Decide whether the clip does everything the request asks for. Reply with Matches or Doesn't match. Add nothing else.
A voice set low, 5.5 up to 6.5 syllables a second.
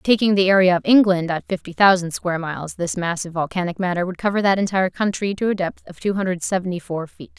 Doesn't match